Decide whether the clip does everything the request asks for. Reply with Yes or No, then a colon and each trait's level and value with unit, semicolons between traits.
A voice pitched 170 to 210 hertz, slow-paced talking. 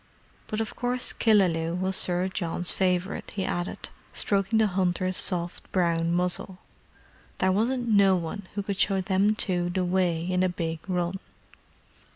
No: medium, 185 Hz; average, 150 wpm